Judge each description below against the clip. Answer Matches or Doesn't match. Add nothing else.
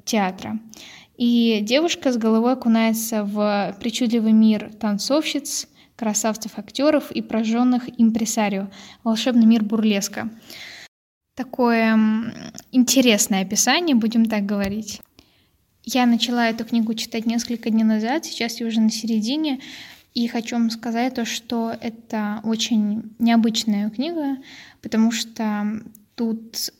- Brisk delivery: Doesn't match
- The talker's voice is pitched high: Matches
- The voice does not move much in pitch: Matches